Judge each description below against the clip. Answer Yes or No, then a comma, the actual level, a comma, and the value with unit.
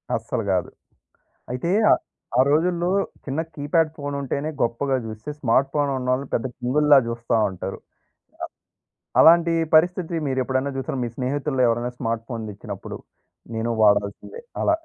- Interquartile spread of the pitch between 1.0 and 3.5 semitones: No, average, 4.2 semitones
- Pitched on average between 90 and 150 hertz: Yes, low, 135 Hz